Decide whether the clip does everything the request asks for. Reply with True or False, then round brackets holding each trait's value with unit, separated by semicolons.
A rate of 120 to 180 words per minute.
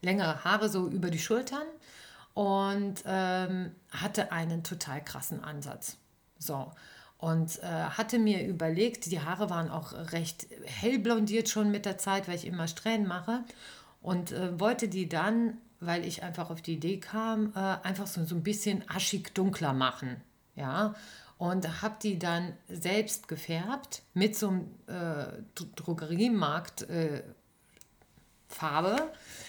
True (140 wpm)